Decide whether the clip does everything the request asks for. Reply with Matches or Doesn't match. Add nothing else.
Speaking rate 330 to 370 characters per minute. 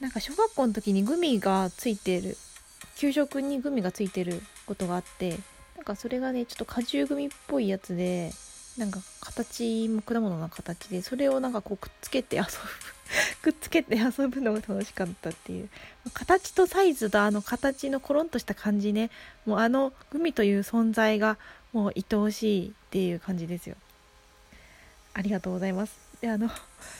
Matches